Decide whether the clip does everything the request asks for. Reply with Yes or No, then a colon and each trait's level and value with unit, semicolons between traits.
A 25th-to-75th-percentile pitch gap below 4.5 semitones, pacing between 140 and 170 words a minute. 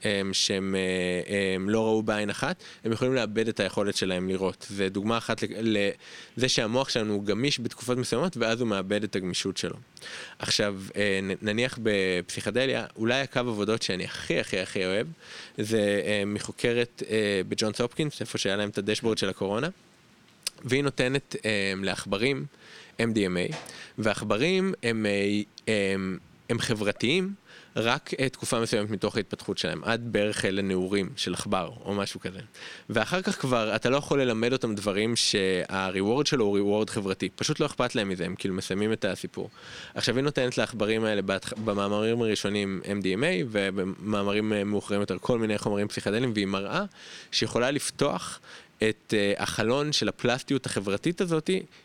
Yes: average, 3.6 semitones; average, 145 wpm